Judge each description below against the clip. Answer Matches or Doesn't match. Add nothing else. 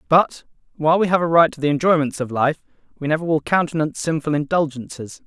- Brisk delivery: Doesn't match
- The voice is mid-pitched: Matches